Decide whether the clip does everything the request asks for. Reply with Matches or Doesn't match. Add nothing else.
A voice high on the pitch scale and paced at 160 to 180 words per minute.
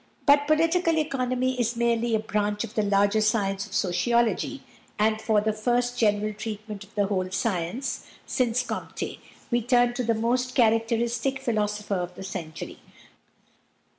Doesn't match